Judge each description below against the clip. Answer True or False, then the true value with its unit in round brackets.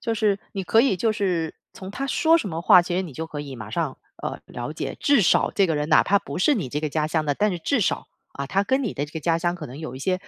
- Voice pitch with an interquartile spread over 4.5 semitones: True (5.0 semitones)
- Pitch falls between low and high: True (175 Hz)